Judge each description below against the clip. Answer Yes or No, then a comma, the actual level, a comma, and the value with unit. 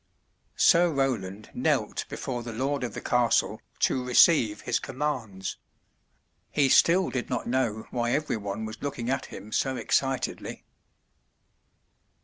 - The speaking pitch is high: No, low, 125 Hz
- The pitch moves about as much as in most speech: Yes, average, 3.5 semitones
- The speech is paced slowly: Yes, slow, 130 wpm